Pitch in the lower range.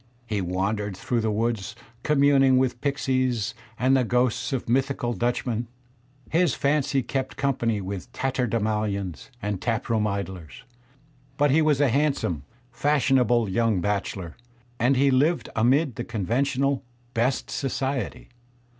Yes: low, 120 Hz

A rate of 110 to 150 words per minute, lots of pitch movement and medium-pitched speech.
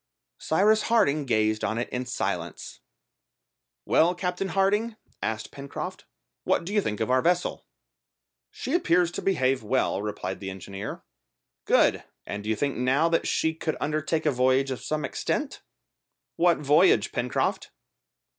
Yes: average, 145 wpm; wide, 6.9 semitones; medium, 145 Hz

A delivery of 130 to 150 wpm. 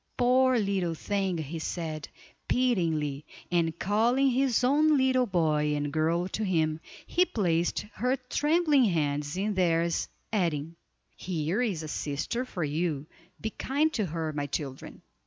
Yes: average, 140 wpm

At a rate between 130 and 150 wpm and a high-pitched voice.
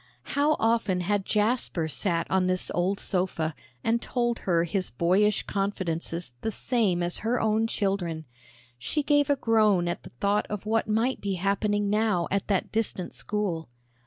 No: average, 160 wpm; high, 200 Hz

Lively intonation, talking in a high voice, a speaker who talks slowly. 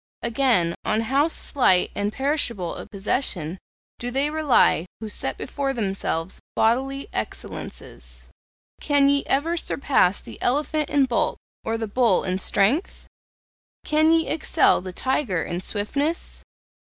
Yes: wide, 6.3 semitones; very high, 250 Hz; slow, 130 wpm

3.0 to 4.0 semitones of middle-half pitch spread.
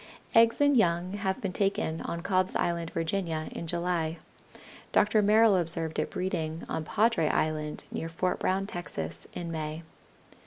Yes: average, 3.4 semitones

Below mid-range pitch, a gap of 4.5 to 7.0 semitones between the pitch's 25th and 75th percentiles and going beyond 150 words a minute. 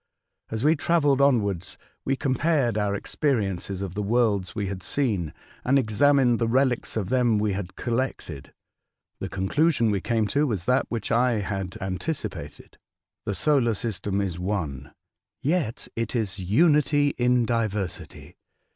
No: low, 115 Hz; average, 5.3 semitones; average, 145 wpm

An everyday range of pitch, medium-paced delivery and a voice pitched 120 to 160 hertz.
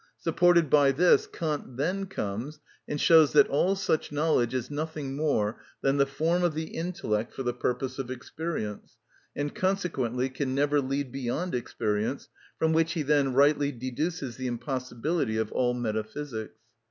Yes: average, 4.3 semitones; average, 155 wpm; medium, 140 Hz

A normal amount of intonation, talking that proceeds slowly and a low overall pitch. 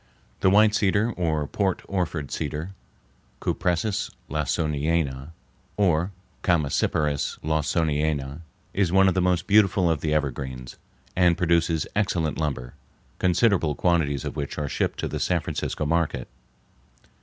Yes: average, 3.6 semitones; slow, 125 wpm; very low, 80 Hz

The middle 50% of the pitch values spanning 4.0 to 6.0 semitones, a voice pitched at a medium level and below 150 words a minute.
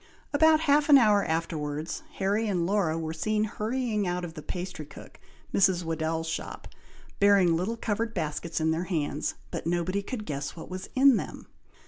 No: average, 4.7 semitones; medium, 180 Hz; average, 170 wpm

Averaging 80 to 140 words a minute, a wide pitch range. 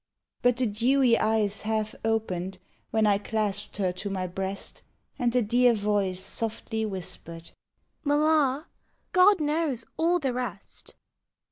No: slow, 135 wpm; average, 4.3 semitones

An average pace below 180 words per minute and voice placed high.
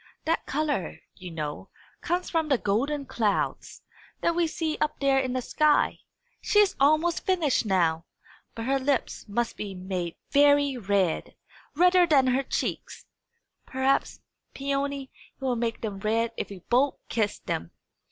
Yes: average, 150 wpm; very high, 265 Hz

